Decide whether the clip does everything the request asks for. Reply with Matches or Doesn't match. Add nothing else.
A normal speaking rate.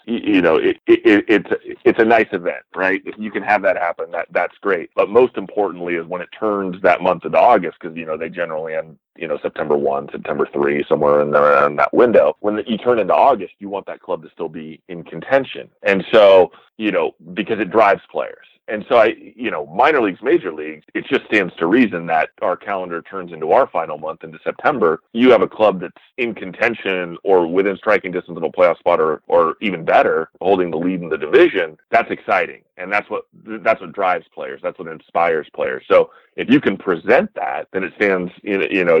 Doesn't match